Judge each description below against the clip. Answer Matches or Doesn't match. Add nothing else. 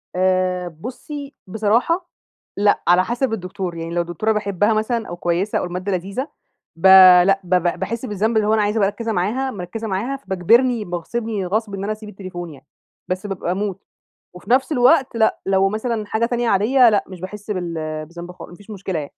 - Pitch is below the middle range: Doesn't match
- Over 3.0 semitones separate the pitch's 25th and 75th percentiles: Matches